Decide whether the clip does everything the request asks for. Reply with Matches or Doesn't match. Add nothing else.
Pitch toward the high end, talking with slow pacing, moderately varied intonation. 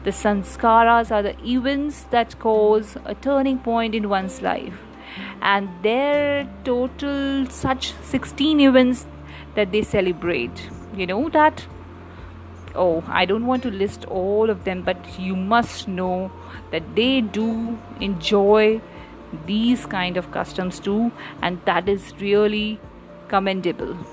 Matches